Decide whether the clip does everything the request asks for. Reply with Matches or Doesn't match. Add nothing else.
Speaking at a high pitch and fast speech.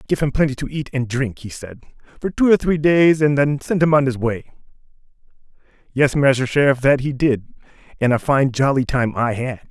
Doesn't match